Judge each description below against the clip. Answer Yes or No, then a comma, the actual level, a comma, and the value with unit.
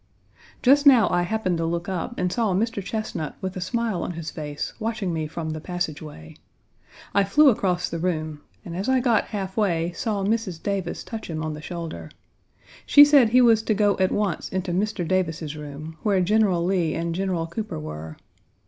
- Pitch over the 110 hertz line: Yes, medium, 185 Hz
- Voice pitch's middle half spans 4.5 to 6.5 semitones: Yes, average, 4.8 semitones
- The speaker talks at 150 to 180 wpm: No, average, 195 wpm